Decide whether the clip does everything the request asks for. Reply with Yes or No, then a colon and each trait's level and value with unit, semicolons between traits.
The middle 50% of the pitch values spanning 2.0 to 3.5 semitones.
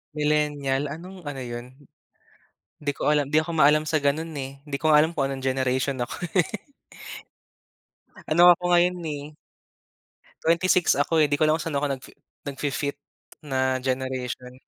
Yes: average, 2.9 semitones